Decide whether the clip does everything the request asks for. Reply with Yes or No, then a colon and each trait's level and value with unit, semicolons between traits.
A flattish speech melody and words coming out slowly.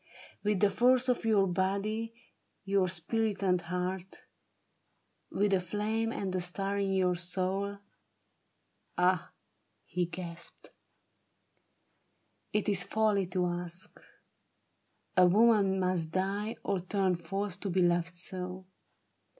Yes: narrow, 2.2 semitones; slow, 125 wpm